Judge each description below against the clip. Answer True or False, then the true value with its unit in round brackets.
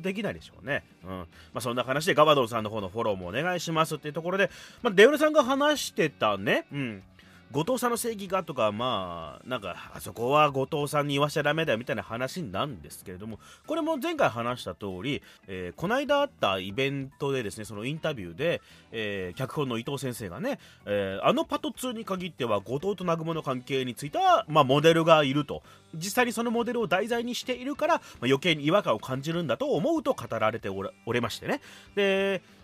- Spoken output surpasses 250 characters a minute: True (430 characters per minute)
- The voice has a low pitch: False (150 Hz)